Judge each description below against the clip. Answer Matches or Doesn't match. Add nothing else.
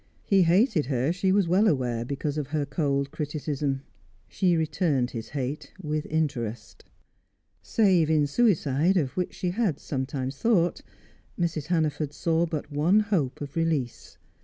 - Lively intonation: Doesn't match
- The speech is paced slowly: Doesn't match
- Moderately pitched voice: Matches